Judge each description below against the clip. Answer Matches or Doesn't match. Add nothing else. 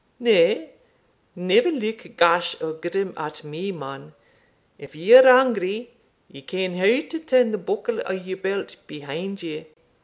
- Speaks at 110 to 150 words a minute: Matches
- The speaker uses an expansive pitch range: Matches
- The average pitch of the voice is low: Doesn't match